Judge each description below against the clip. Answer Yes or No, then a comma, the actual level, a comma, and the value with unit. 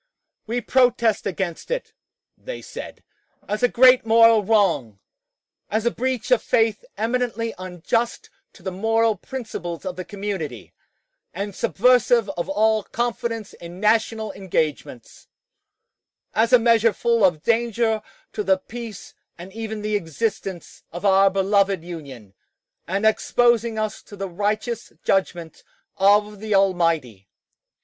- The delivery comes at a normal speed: No, slow, 130 wpm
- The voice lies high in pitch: Yes, high, 210 Hz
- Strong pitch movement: No, average, 3.6 semitones